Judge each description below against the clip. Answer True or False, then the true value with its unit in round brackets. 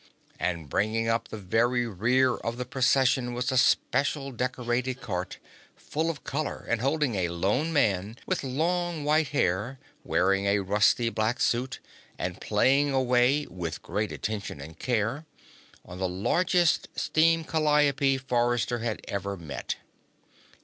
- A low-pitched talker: True (120 Hz)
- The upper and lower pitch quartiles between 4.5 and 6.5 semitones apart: True (5.1 semitones)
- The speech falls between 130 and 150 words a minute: True (140 wpm)